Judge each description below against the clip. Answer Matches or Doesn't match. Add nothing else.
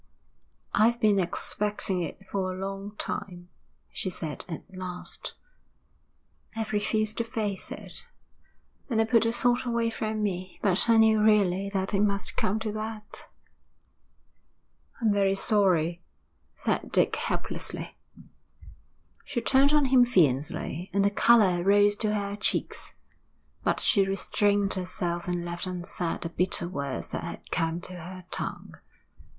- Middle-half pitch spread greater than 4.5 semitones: Doesn't match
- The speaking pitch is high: Matches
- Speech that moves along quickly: Doesn't match